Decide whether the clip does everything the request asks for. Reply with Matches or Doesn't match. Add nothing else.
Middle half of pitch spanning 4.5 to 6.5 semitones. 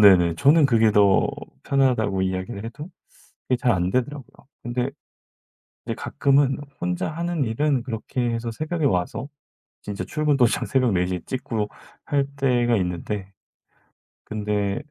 Matches